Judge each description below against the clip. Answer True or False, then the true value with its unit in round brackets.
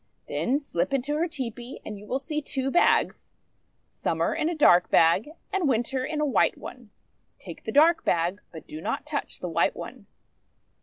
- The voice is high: True (265 Hz)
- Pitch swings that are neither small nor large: False (6.6 semitones)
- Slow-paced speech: False (190 wpm)